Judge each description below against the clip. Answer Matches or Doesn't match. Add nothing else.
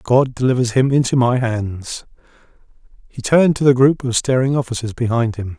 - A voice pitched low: Matches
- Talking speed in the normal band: Matches